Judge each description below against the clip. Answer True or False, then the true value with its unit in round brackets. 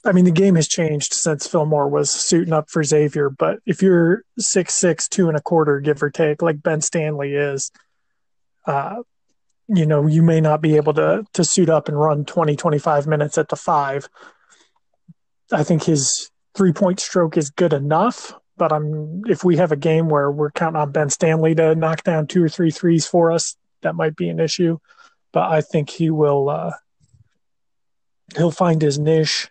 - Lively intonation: False (2.6 semitones)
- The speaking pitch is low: False (160 Hz)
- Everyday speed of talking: True (195 wpm)